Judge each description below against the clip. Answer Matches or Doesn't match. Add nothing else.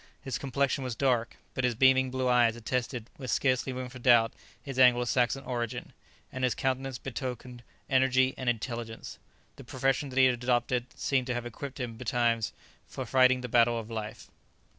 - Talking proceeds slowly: Doesn't match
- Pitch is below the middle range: Matches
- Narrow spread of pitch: Matches